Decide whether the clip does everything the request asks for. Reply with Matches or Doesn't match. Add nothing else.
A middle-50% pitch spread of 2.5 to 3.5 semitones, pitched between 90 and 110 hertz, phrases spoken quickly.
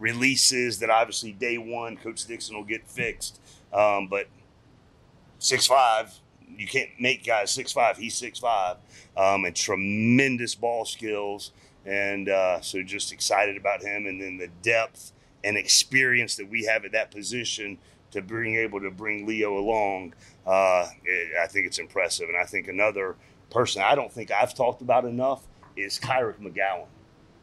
Doesn't match